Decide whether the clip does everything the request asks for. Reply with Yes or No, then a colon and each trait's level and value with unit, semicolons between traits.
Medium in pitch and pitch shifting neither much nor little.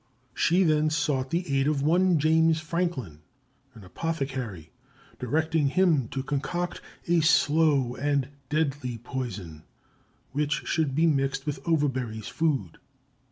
Yes: medium, 145 Hz; average, 3.6 semitones